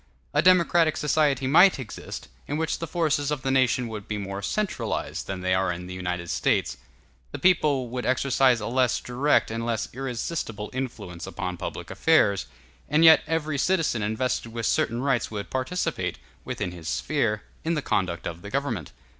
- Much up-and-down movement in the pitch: Yes, wide, 6.4 semitones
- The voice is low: Yes, low, 125 Hz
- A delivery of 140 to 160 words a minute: No, average, 175 wpm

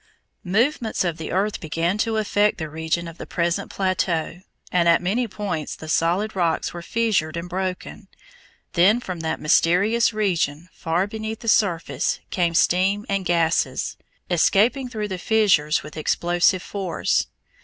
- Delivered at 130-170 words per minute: Yes, average, 150 wpm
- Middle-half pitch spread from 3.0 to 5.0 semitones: Yes, average, 3.8 semitones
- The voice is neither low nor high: Yes, medium, 180 Hz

